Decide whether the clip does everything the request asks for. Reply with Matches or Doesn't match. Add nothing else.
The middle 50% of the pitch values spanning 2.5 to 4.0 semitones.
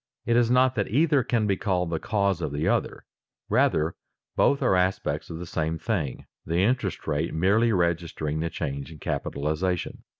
Doesn't match